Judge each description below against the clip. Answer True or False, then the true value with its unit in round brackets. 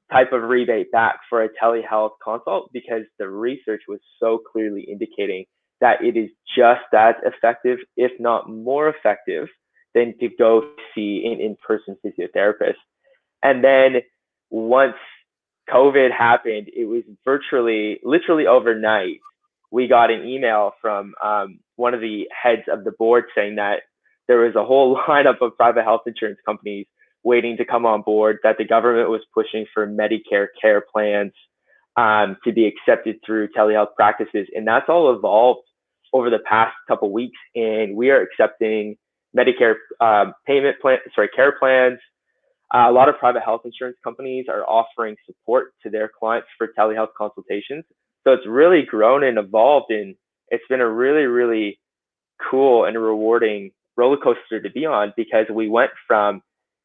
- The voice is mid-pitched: False (115 Hz)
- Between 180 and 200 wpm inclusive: False (160 wpm)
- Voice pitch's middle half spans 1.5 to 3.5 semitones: False (3.9 semitones)